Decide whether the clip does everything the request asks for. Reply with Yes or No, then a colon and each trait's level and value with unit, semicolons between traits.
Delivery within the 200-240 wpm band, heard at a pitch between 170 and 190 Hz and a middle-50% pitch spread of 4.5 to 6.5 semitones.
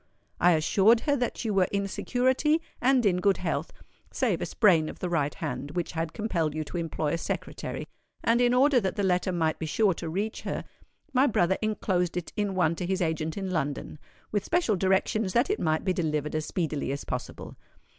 Yes: fast, 205 wpm; medium, 185 Hz; average, 5.1 semitones